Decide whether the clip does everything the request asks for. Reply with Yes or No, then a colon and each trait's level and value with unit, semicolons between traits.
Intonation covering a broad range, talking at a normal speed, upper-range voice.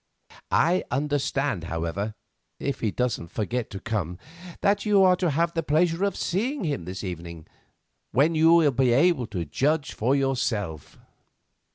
No: wide, 8.6 semitones; average, 145 wpm; low, 135 Hz